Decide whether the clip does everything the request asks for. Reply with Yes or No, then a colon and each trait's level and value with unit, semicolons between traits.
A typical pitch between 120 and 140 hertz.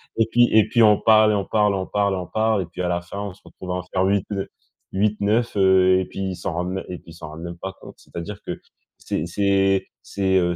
No: very low, 95 Hz